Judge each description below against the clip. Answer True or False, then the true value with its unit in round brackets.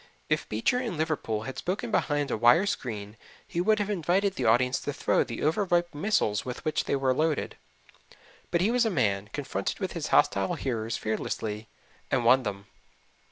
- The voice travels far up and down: True (8.0 semitones)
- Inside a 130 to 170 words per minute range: False (180 wpm)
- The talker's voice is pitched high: False (140 Hz)